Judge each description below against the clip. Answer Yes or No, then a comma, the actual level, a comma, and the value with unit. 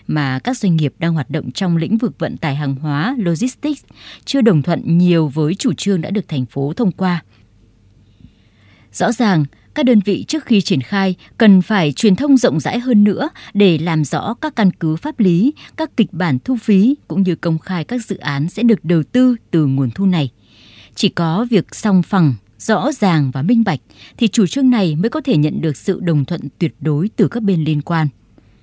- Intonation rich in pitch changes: Yes, wide, 6.8 semitones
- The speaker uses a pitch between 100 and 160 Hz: No, medium, 180 Hz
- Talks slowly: No, average, 215 wpm